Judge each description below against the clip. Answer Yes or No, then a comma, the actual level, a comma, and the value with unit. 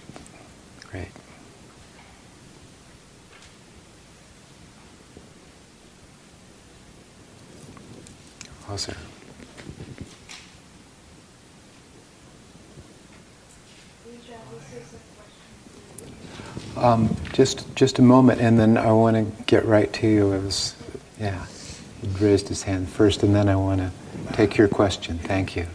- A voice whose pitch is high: No, low, 105 Hz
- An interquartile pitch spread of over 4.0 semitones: No, average, 3.1 semitones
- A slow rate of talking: Yes, slow, 75 wpm